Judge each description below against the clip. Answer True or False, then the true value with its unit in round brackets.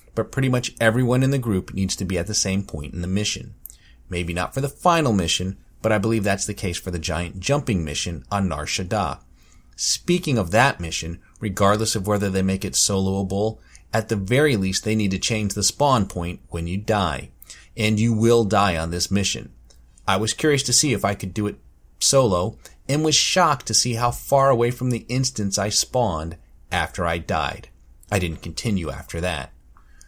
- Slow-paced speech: False (200 wpm)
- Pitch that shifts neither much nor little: True (4.7 semitones)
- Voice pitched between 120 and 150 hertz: False (100 Hz)